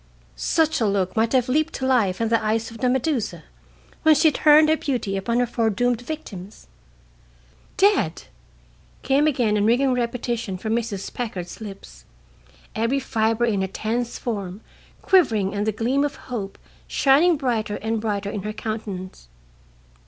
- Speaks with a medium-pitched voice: No, high, 230 Hz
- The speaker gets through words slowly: No, average, 155 wpm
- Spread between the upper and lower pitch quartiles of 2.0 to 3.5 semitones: No, average, 4.1 semitones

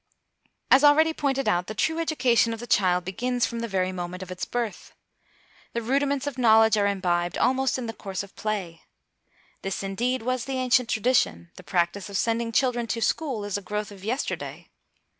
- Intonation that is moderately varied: Yes, average, 4.8 semitones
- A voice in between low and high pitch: No, high, 225 Hz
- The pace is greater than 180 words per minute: Yes, average, 190 wpm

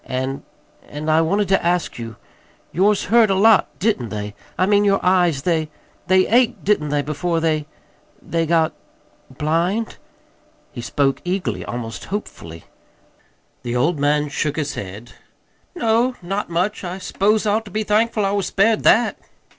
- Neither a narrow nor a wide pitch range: No, wide, 5.8 semitones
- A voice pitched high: No, medium, 175 Hz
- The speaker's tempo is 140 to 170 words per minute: Yes, average, 160 wpm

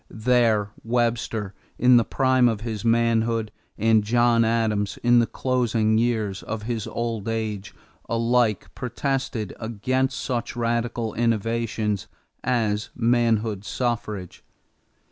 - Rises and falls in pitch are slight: Yes, narrow, 1.8 semitones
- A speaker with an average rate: No, slow, 110 wpm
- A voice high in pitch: No, low, 115 Hz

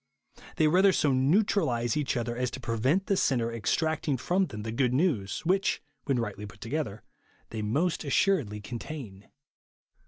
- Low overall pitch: Yes, low, 130 Hz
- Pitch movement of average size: No, wide, 6.0 semitones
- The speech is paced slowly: No, average, 160 wpm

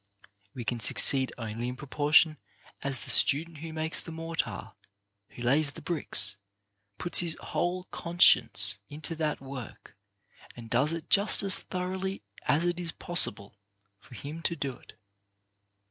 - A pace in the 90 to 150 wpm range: Yes, average, 145 wpm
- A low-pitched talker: No, medium, 155 Hz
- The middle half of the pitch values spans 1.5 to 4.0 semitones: No, average, 4.7 semitones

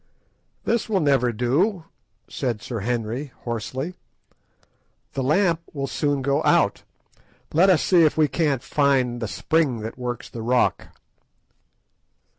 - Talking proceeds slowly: Yes, slow, 130 wpm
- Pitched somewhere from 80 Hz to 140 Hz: Yes, low, 135 Hz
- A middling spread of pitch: Yes, average, 4.6 semitones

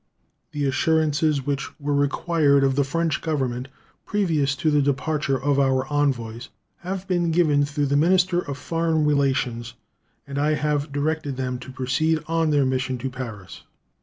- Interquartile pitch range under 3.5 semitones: Yes, average, 3.0 semitones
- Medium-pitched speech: Yes, medium, 145 Hz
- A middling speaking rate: Yes, average, 160 wpm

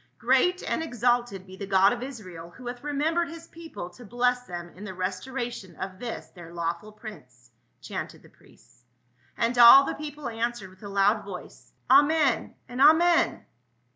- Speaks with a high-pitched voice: Yes, high, 235 Hz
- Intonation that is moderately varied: No, wide, 6.2 semitones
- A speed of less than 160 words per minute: No, average, 180 wpm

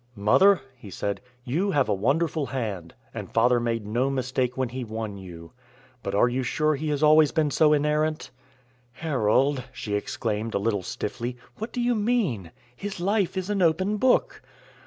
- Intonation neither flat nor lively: No, wide, 6.1 semitones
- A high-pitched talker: No, low, 130 Hz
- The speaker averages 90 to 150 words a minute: No, average, 175 wpm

